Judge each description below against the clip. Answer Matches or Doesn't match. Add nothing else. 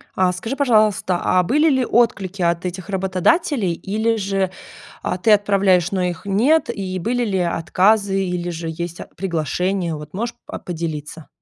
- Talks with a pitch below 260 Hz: Matches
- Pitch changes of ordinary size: Matches